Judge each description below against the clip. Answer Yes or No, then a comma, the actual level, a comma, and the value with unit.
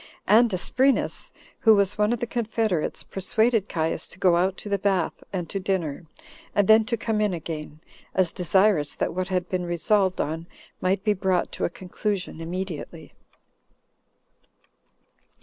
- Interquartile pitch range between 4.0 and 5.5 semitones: No, average, 3.3 semitones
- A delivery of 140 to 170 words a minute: Yes, average, 155 wpm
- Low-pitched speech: No, high, 190 Hz